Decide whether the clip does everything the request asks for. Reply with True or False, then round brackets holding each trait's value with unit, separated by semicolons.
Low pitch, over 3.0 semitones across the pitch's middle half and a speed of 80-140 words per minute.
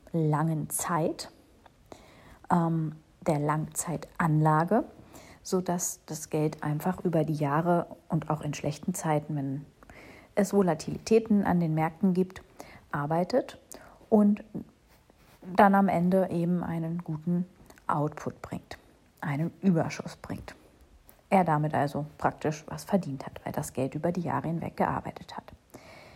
False (165 Hz; 3.4 semitones; 125 wpm)